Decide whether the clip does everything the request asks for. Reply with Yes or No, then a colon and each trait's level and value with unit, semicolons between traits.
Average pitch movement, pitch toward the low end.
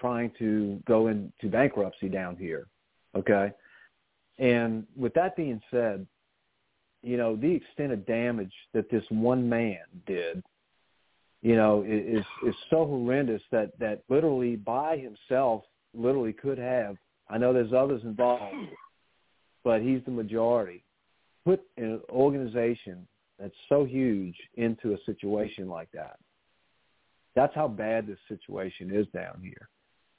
Yes: average, 3.0 semitones; low, 115 Hz